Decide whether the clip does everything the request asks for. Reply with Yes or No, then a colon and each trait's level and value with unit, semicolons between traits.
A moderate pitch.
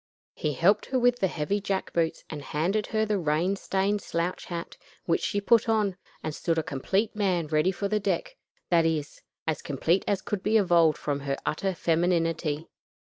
Yes: medium, 180 Hz